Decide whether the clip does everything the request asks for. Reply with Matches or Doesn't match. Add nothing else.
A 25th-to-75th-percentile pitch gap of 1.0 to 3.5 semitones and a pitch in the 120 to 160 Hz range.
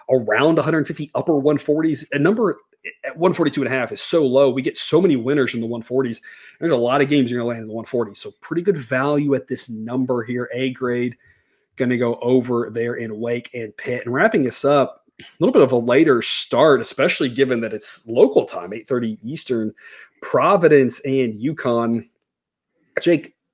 Matches